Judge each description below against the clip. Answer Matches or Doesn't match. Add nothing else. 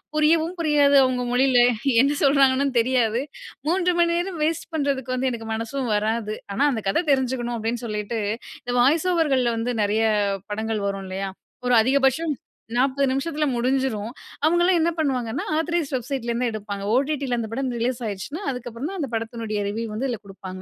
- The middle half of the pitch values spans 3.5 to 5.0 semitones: Matches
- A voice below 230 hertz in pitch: Doesn't match